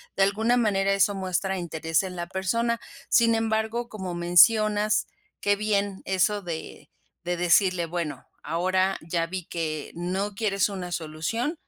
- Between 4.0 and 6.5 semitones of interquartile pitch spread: No, average, 3.4 semitones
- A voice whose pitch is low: No, high, 190 Hz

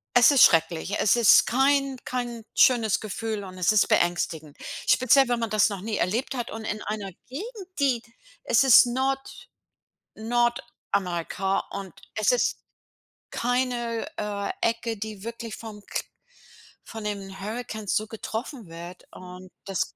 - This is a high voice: Yes, high, 220 Hz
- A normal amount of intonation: Yes, average, 3.6 semitones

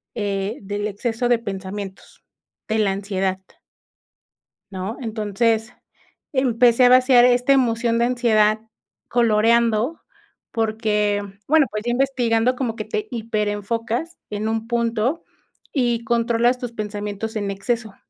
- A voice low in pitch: No, high, 225 Hz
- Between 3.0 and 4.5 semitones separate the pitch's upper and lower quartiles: No, narrow, 2.5 semitones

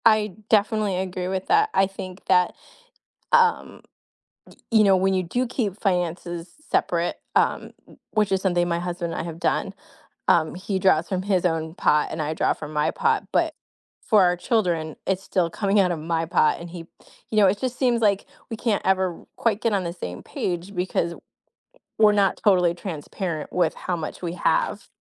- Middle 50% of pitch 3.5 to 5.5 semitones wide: No, average, 3.1 semitones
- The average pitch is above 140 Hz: Yes, medium, 185 Hz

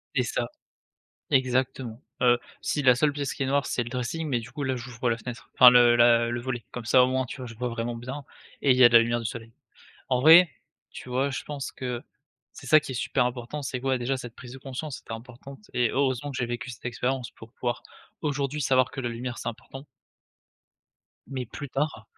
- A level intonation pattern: Yes, narrow, 2.0 semitones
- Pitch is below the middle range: Yes, low, 125 Hz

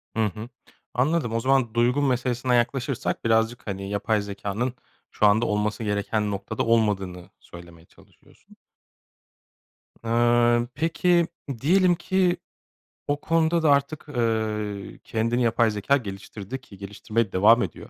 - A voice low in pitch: Yes, low, 115 Hz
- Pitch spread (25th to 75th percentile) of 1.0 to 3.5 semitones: No, average, 3.9 semitones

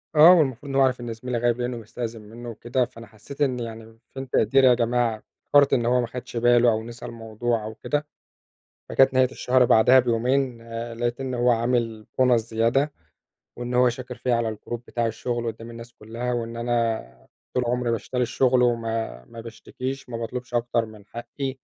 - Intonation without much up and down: Yes, narrow, 1.6 semitones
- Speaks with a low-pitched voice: Yes, low, 120 Hz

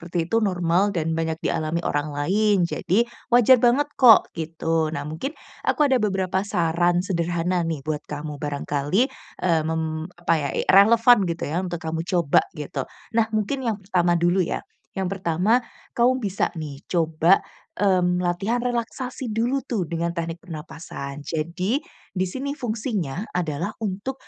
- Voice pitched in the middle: Yes, medium, 180 Hz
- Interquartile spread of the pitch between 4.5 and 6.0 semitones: Yes, average, 4.8 semitones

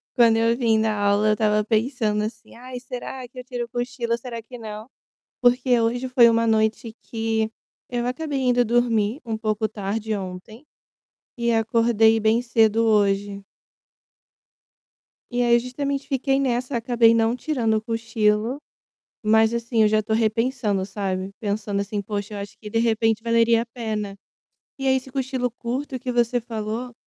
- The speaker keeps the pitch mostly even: Yes, narrow, 2.3 semitones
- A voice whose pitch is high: Yes, high, 230 Hz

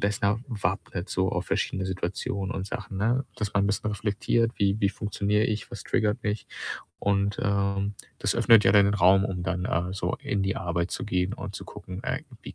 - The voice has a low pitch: Yes, low, 100 Hz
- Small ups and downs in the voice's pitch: Yes, narrow, 1.7 semitones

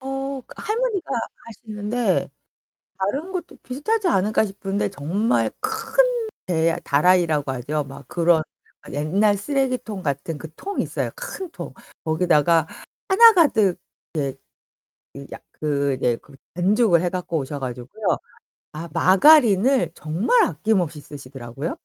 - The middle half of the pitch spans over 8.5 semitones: Yes, wide, 9.0 semitones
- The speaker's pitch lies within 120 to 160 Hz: No, medium, 185 Hz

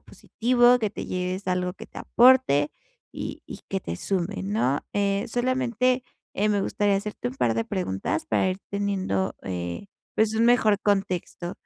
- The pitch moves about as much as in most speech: Yes, average, 3.6 semitones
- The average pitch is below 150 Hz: No, high, 200 Hz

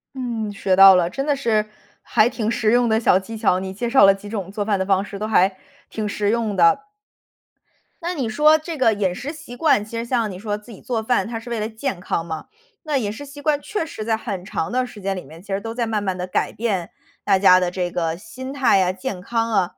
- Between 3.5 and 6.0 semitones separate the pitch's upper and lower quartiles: Yes, average, 4.0 semitones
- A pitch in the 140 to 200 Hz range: No, high, 215 Hz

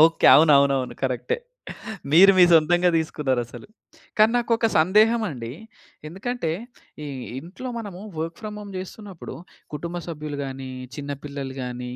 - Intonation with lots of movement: Yes, wide, 5.9 semitones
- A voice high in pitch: No, medium, 160 Hz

